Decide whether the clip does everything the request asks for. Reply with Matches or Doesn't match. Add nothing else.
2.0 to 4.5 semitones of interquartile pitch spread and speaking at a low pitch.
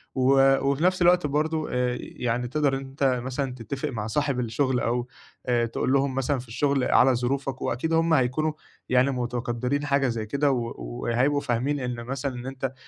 Matches